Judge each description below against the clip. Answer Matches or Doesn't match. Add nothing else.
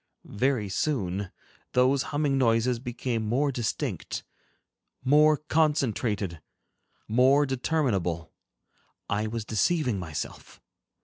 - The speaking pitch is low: Matches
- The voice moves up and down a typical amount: Matches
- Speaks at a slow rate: Matches